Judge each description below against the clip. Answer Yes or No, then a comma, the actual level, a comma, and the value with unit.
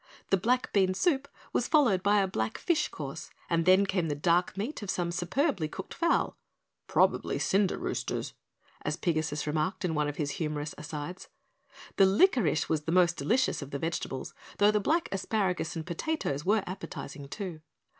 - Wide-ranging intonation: No, average, 4.8 semitones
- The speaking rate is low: No, average, 170 wpm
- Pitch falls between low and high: Yes, medium, 180 Hz